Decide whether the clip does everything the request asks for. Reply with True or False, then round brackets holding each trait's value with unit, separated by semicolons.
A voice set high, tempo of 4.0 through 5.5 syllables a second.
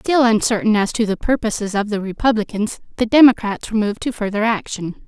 False (220 Hz; 6.0 syllables/s)